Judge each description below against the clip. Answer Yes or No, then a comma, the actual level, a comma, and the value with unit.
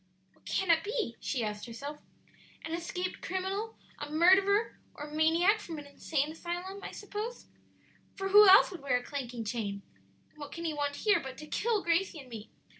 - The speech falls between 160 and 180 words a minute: No, average, 190 wpm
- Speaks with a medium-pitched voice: No, very high, 330 Hz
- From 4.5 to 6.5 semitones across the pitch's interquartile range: Yes, average, 5.3 semitones